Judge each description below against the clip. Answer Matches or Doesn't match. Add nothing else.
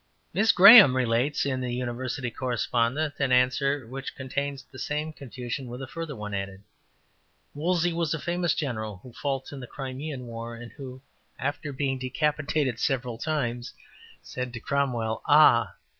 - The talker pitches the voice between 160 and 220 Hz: Doesn't match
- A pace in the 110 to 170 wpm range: Matches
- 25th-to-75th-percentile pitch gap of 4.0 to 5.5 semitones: Doesn't match